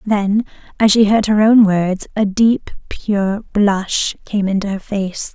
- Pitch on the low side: No, high, 205 Hz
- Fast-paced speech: No, average, 170 wpm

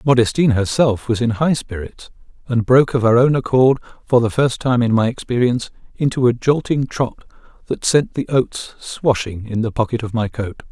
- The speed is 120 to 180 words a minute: No, average, 190 wpm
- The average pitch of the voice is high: No, low, 120 Hz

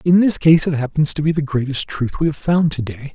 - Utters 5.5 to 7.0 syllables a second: Yes, 5.6 syllables/s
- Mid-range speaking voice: Yes, medium, 150 Hz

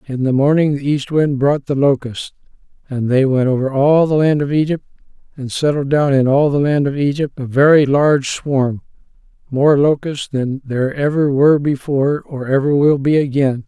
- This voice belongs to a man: Yes, male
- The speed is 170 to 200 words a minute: Yes, average, 190 wpm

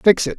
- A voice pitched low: No, high, 190 Hz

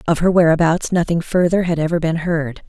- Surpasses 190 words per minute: Yes, average, 200 wpm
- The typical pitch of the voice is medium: Yes, medium, 165 Hz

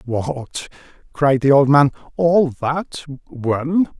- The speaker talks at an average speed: No, slow, 90 wpm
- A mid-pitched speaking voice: Yes, medium, 145 Hz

